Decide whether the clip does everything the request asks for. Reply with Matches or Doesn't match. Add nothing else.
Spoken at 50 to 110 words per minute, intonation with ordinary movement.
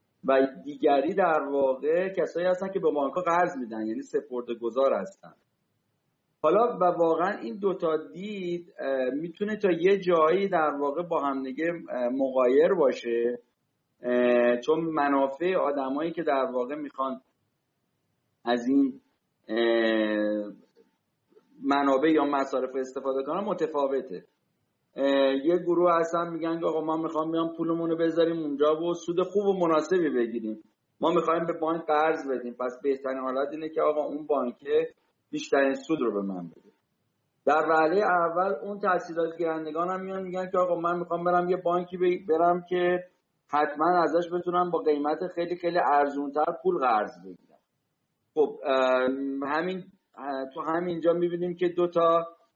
Doesn't match